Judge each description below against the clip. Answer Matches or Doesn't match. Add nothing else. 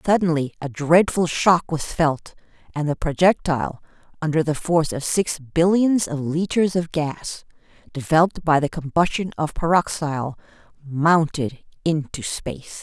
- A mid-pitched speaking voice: Matches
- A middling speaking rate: Doesn't match